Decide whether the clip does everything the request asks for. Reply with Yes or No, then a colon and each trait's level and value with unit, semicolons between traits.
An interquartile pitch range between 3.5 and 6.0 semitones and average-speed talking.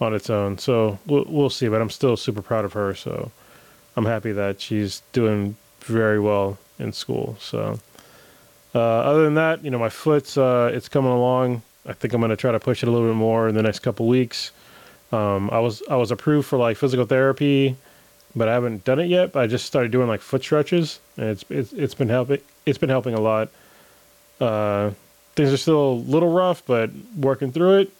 No: average, 4.1 semitones; fast, 215 wpm